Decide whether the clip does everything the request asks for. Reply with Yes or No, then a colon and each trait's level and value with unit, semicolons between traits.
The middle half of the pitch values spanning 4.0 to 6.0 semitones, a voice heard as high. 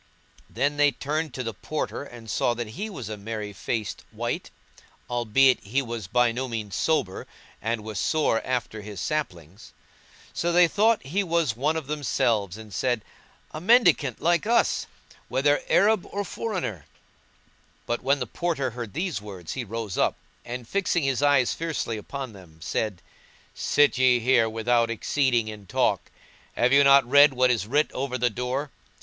No: average, 5.0 semitones; low, 125 Hz